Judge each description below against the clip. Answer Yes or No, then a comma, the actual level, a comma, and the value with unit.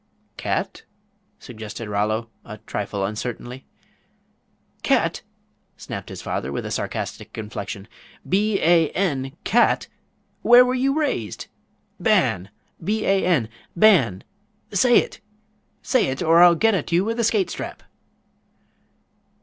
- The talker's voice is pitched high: No, medium, 165 Hz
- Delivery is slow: Yes, slow, 125 wpm